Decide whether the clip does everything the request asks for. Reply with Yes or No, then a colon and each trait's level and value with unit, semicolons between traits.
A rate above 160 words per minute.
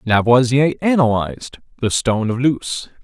No: slow, 120 wpm